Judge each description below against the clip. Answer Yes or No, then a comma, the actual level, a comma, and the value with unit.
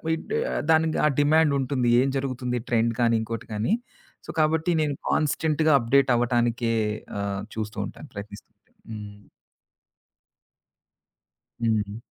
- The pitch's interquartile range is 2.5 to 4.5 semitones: No, average, 5.0 semitones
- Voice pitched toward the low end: Yes, low, 120 Hz